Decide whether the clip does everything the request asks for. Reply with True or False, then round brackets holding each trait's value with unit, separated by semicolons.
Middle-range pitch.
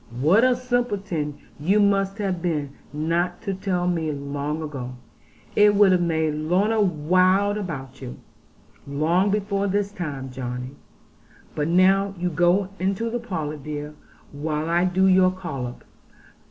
True (175 Hz)